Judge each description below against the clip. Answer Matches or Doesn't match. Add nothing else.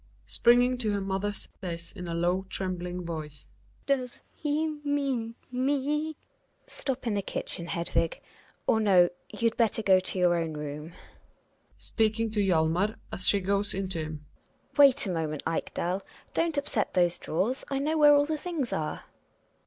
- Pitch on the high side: Matches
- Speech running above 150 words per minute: Matches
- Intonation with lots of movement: Matches